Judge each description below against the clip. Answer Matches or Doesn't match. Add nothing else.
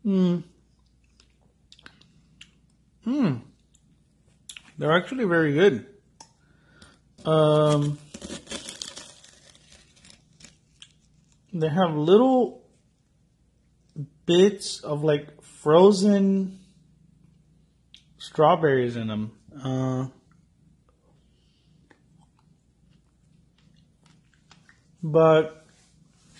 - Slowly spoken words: Matches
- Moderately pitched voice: Matches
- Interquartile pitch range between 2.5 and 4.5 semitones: Matches